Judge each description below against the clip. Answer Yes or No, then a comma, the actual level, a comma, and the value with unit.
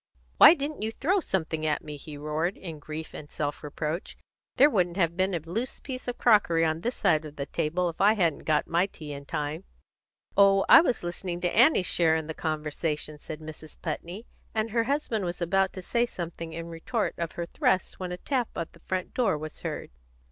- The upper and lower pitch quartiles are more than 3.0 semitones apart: Yes, average, 4.5 semitones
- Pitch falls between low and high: Yes, medium, 170 Hz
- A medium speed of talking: No, fast, 215 wpm